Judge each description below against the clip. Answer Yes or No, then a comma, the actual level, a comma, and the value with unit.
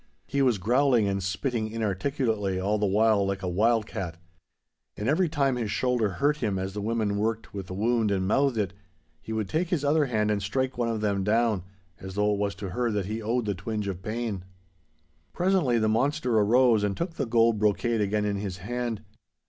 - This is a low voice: Yes, low, 110 Hz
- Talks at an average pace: No, fast, 210 wpm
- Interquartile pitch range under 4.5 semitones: Yes, average, 3.3 semitones